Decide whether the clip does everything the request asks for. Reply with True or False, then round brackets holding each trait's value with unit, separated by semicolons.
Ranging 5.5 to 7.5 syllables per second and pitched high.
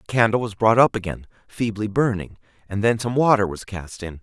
False (5.6 syllables/s; 105 Hz)